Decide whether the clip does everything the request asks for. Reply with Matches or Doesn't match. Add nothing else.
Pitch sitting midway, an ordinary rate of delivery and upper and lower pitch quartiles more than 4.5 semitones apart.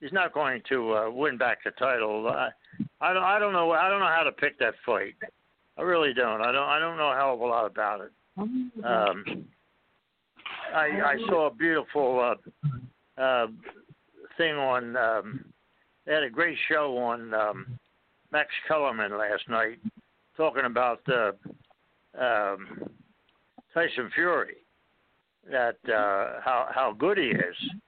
Matches